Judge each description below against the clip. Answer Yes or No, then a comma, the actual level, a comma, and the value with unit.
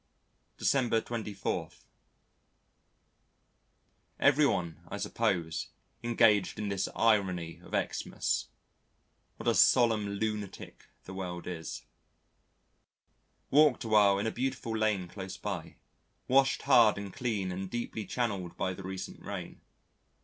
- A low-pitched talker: Yes, low, 105 Hz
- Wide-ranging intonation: No, average, 3.7 semitones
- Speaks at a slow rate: Yes, slow, 110 wpm